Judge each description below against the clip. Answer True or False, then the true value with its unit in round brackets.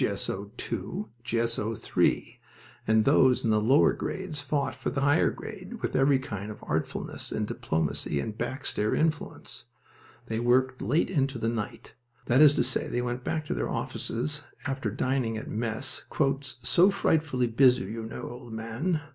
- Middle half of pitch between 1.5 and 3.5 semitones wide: False (4.2 semitones)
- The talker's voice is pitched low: True (125 Hz)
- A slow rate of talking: False (165 wpm)